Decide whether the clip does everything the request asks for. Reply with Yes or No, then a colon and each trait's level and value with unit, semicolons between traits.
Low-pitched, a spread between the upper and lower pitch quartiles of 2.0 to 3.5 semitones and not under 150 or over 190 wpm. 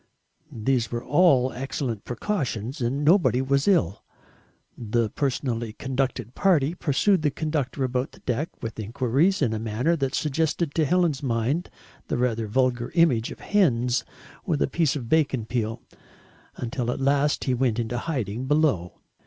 No: low, 130 Hz; average, 4.2 semitones; average, 155 wpm